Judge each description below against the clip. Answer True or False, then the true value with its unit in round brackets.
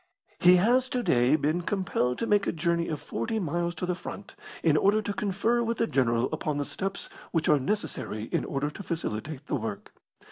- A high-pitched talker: False (170 Hz)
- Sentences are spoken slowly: False (205 wpm)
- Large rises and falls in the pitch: True (6.1 semitones)